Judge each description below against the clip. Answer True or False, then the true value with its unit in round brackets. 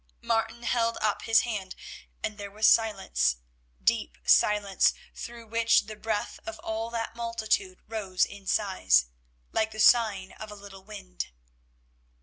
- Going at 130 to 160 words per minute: True (140 wpm)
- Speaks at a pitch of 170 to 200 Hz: False (215 Hz)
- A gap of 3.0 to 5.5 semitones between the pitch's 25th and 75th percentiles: False (2.6 semitones)